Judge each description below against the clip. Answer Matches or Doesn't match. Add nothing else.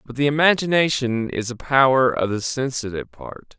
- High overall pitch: Doesn't match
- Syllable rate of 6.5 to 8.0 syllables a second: Doesn't match